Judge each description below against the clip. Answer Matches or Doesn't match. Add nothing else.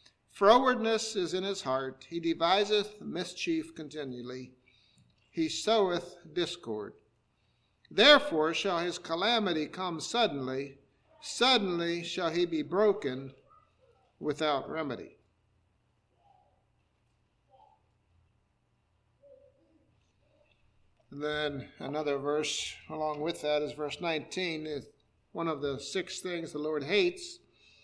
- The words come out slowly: Matches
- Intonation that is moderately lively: Doesn't match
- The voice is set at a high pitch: Doesn't match